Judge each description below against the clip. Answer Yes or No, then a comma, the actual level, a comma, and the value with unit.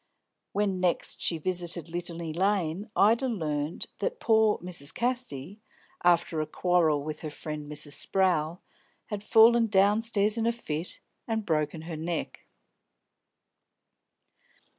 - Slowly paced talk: Yes, slow, 120 wpm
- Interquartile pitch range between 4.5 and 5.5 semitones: Yes, average, 5.1 semitones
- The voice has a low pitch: No, medium, 175 Hz